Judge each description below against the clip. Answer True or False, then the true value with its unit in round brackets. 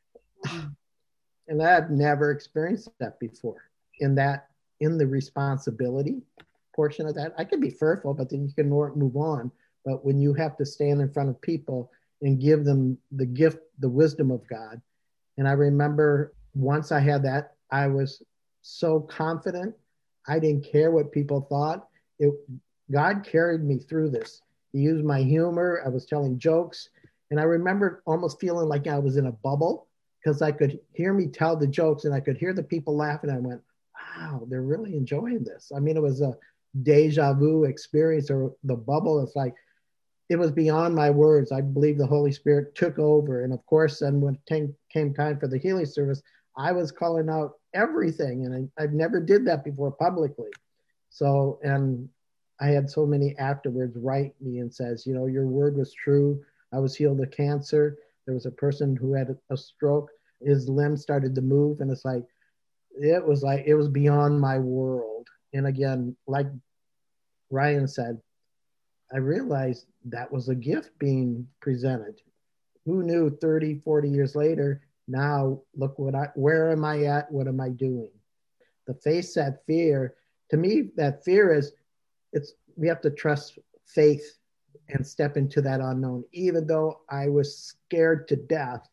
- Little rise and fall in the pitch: True (2.2 semitones)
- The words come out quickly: False (180 wpm)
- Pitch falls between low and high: True (145 Hz)